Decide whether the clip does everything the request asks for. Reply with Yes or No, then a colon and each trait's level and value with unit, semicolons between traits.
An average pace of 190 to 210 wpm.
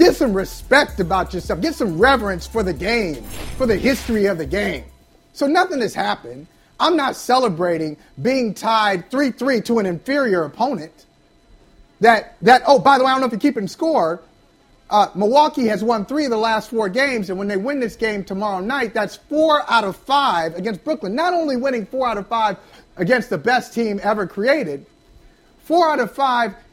Yes: average, 200 wpm